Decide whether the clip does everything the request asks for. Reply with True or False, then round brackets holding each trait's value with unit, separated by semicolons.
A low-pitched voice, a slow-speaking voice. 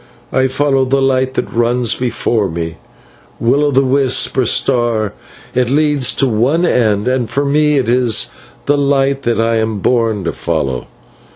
False (125 Hz; 170 wpm)